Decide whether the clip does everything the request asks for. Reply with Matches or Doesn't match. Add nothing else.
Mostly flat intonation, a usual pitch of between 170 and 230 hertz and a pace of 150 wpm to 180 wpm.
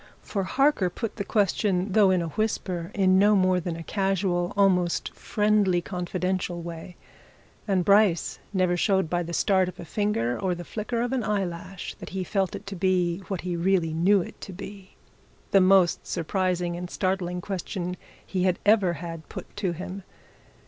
Matches